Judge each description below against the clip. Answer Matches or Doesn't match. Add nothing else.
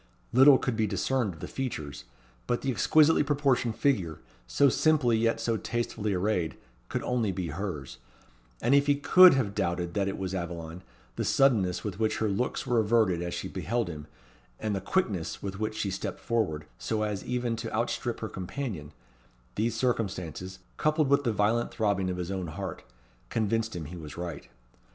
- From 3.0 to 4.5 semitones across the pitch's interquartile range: Doesn't match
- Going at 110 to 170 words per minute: Doesn't match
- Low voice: Matches